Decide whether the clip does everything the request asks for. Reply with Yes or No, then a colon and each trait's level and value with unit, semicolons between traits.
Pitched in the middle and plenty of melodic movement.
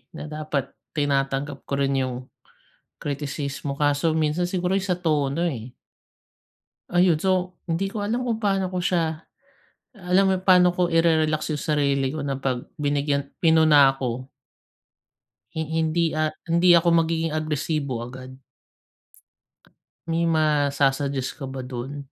No: medium, 155 Hz; average, 3.7 semitones